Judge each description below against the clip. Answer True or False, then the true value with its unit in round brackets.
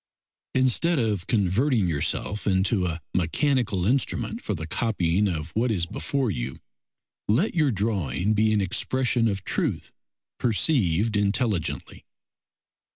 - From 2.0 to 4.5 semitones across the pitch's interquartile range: False (5.2 semitones)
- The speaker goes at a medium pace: False (120 wpm)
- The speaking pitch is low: True (105 Hz)